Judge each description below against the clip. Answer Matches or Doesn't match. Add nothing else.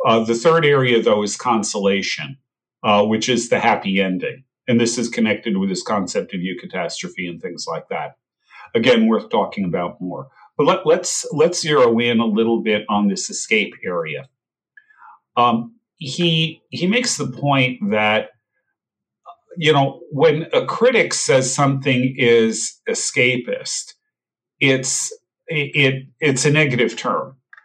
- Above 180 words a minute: Doesn't match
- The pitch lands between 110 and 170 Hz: Matches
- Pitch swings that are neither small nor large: Doesn't match